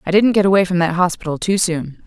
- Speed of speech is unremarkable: No, fast, 260 wpm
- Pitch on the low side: No, medium, 180 Hz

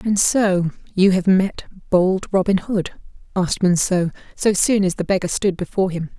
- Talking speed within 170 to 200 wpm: Yes, average, 175 wpm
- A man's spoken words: No, female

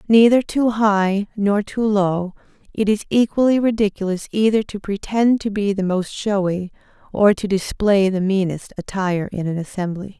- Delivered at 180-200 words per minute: No, average, 160 wpm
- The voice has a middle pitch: No, high, 200 Hz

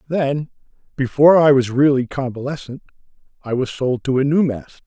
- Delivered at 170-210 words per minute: No, average, 160 wpm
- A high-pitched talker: No, low, 135 Hz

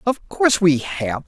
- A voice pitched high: No, medium, 165 Hz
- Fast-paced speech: No, average, 190 wpm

